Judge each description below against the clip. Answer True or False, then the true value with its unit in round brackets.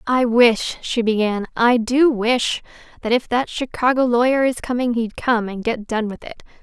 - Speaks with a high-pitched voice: True (235 Hz)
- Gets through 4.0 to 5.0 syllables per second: True (4.5 syllables/s)